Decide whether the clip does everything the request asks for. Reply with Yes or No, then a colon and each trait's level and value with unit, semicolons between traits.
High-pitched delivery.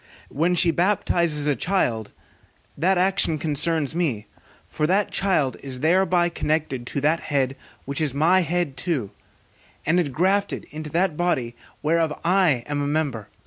No: medium, 155 Hz